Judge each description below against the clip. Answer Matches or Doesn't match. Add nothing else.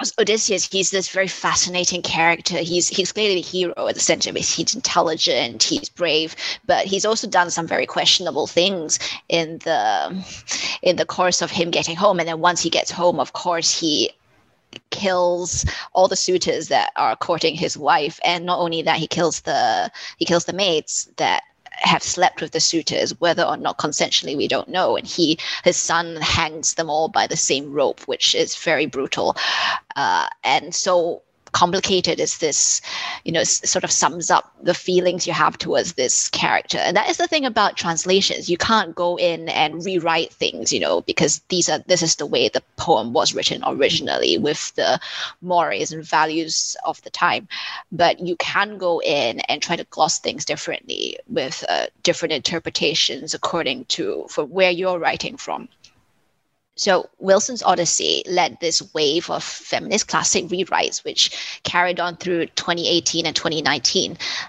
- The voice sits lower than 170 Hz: Doesn't match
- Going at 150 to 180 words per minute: Matches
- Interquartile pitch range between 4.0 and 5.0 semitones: Doesn't match